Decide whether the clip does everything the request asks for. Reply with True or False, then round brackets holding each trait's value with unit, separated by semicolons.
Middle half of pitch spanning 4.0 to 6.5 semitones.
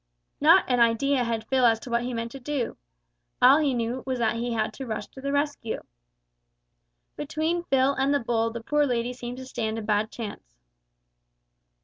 False (3.0 semitones)